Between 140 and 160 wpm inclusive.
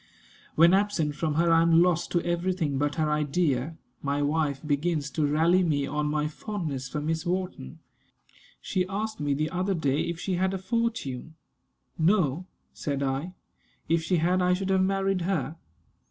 No: average, 175 wpm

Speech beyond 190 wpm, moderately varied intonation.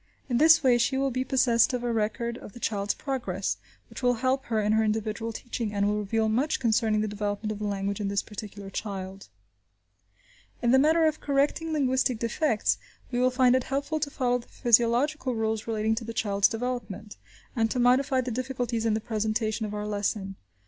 Yes: average, 200 wpm; average, 3.3 semitones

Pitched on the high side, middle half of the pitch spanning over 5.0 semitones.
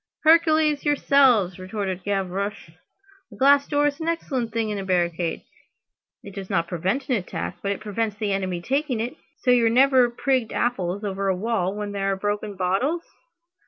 Yes: high, 210 Hz; wide, 5.6 semitones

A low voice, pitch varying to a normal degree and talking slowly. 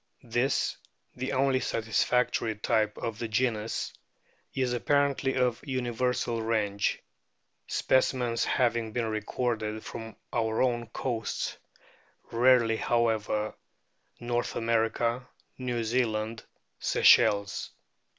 No: low, 115 Hz; narrow, 2.1 semitones; slow, 95 wpm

